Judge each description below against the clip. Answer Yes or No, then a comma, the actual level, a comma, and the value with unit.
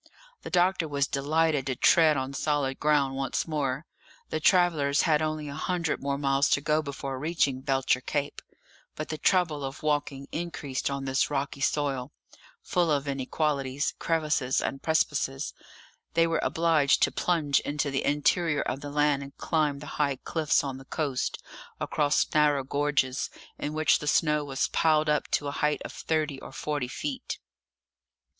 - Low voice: No, medium, 145 Hz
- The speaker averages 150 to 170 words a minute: Yes, average, 165 wpm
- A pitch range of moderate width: No, narrow, 2.1 semitones